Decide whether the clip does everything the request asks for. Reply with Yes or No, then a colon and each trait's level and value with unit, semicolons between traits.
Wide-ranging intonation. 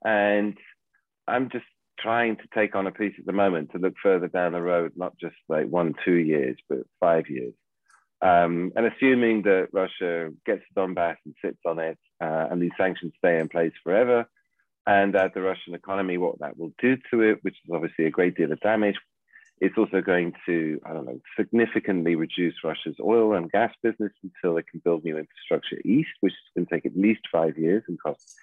No: average, 4.0 semitones